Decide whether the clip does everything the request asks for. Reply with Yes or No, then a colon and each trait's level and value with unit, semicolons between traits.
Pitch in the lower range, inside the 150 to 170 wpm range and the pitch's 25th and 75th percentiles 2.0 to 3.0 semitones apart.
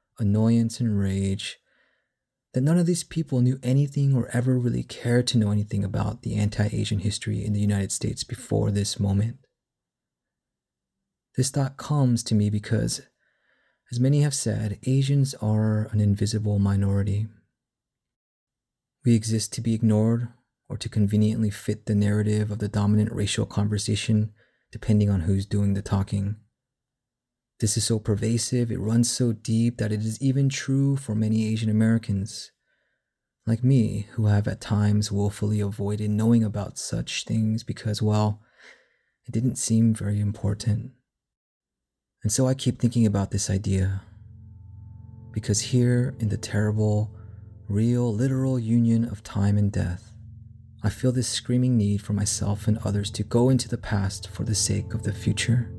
Yes: low, 110 Hz; average, 155 wpm; narrow, 2.5 semitones